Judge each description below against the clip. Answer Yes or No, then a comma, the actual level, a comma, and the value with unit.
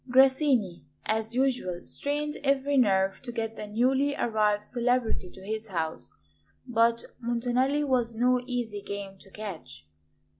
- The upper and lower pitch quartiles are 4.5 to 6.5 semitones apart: No, average, 4.0 semitones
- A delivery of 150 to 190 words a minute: No, slow, 135 wpm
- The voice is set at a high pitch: Yes, high, 230 Hz